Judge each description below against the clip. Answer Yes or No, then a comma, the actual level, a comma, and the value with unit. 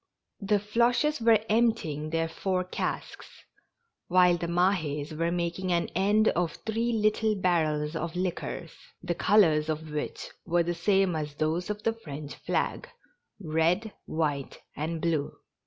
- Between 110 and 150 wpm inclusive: Yes, average, 145 wpm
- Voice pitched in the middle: Yes, medium, 175 Hz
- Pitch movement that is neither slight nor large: Yes, average, 4.7 semitones